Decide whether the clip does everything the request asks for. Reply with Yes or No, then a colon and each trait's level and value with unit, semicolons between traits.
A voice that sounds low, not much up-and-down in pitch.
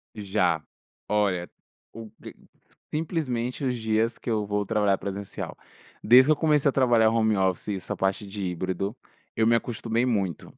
No: low, 110 Hz; average, 3.5 semitones